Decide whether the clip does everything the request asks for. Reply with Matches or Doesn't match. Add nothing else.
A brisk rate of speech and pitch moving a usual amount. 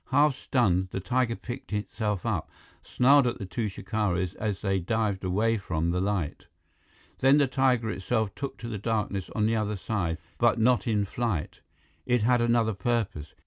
Doesn't match